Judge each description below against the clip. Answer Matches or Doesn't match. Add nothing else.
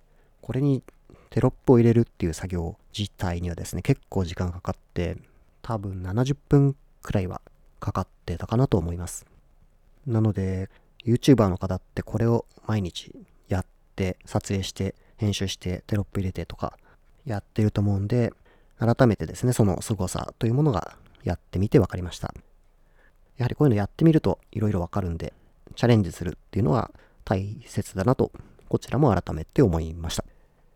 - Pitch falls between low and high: Doesn't match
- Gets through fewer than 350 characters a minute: Doesn't match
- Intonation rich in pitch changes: Doesn't match